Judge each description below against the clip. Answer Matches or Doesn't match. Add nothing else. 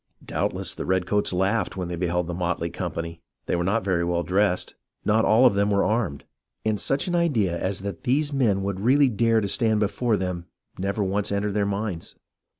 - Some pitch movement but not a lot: Matches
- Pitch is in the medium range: Doesn't match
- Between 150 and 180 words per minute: Doesn't match